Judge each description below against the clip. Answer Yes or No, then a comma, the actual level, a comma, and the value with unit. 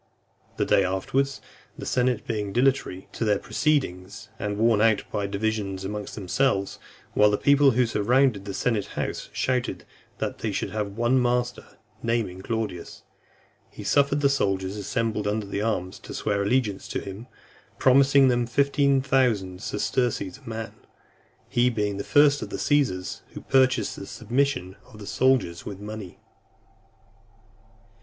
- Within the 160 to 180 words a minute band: No, average, 150 wpm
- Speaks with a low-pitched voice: Yes, low, 110 Hz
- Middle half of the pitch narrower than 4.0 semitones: No, average, 4.5 semitones